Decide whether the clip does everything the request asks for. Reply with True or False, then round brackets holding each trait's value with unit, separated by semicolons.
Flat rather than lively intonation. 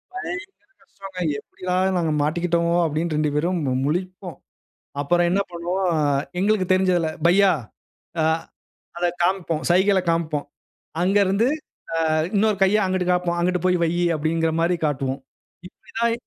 True (2.3 semitones)